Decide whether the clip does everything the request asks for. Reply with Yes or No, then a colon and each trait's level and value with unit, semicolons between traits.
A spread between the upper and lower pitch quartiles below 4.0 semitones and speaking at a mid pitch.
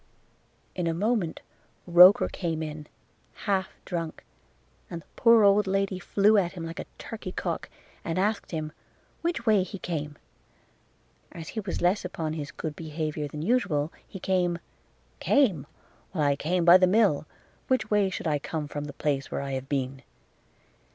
No: average, 4.4 semitones; medium, 175 Hz